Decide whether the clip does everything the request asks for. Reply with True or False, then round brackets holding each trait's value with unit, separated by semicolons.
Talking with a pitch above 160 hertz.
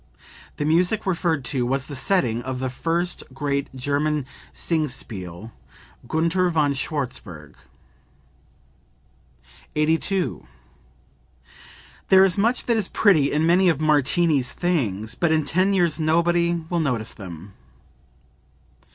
False (155 Hz)